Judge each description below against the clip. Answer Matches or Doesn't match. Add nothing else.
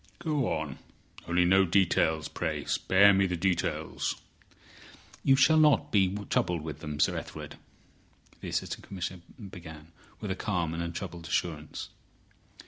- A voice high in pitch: Doesn't match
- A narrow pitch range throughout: Doesn't match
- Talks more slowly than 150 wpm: Matches